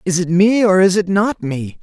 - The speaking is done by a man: Yes, male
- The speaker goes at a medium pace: No, fast, 260 wpm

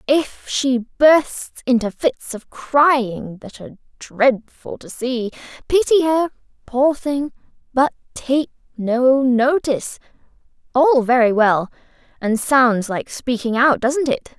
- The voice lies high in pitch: Yes, very high, 255 Hz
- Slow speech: Yes, slow, 125 wpm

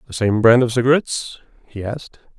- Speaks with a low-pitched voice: Yes, low, 120 Hz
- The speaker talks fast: No, average, 175 wpm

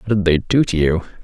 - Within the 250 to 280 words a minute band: No, fast, 290 wpm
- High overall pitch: No, very low, 95 Hz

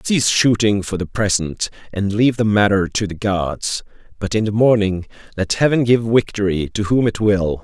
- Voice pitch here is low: Yes, low, 105 Hz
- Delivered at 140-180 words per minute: No, average, 190 wpm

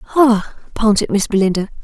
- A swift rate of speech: No, slow, 130 wpm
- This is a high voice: Yes, high, 215 Hz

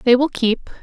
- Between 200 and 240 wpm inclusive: Yes, fast, 220 wpm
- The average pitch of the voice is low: No, very high, 250 Hz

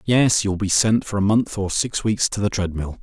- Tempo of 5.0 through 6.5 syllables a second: No, 4.8 syllables/s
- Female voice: No, male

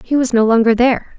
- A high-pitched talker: Yes, high, 240 Hz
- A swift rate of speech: Yes, fast, 255 wpm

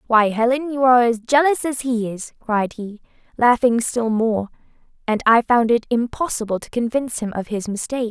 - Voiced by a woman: Yes, female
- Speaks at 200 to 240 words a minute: No, average, 185 wpm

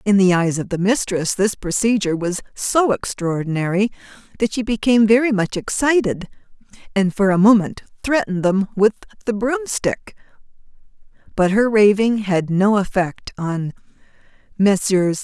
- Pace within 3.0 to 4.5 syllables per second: No, 4.7 syllables/s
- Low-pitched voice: No, high, 200 Hz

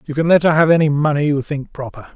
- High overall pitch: No, medium, 150 Hz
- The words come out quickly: Yes, fast, 280 wpm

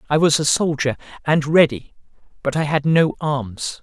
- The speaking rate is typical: Yes, average, 175 wpm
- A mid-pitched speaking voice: Yes, medium, 145 Hz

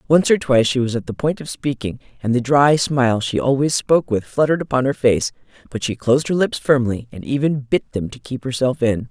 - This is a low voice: Yes, low, 130 Hz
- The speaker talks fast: Yes, fast, 235 wpm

